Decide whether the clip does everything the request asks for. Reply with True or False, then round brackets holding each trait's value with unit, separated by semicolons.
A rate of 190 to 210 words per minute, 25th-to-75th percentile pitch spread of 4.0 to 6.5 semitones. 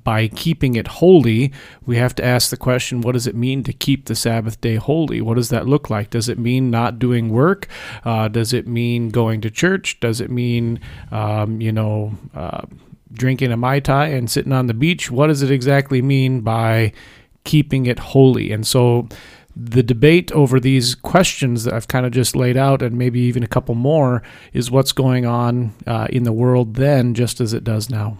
False (205 wpm; 2.4 semitones)